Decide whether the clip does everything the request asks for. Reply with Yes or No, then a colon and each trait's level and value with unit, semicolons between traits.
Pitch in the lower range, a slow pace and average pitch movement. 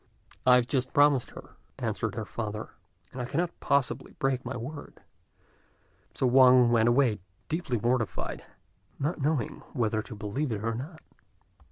No: low, 125 Hz; average, 150 wpm; average, 3.5 semitones